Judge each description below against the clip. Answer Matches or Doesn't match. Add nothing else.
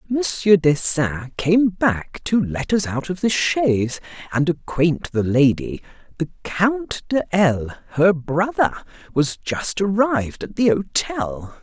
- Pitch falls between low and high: Matches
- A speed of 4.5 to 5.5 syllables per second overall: Doesn't match